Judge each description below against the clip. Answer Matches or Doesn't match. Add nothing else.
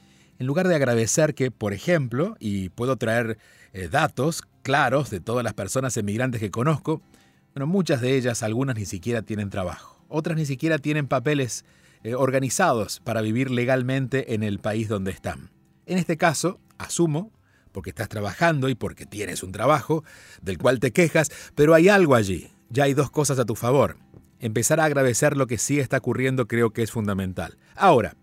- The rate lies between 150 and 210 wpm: Matches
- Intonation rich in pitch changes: Matches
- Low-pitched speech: Matches